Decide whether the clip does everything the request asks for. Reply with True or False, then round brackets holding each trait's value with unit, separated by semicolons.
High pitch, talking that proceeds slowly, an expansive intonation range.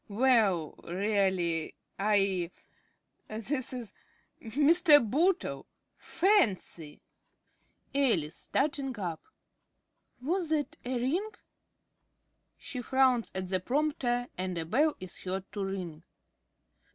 True (230 Hz; 95 wpm; 7.0 semitones)